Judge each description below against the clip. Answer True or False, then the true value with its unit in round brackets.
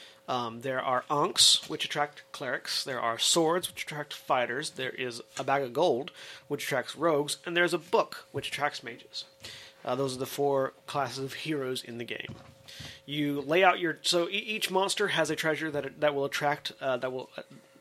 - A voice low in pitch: False (145 Hz)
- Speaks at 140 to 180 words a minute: False (200 wpm)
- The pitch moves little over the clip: False (3.8 semitones)